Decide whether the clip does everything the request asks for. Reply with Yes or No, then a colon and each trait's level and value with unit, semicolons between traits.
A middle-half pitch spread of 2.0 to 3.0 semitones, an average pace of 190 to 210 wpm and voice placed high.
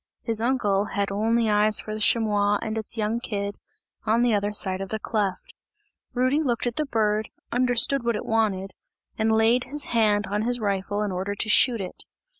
Yes: narrow, 2.4 semitones; average, 195 wpm; high, 215 Hz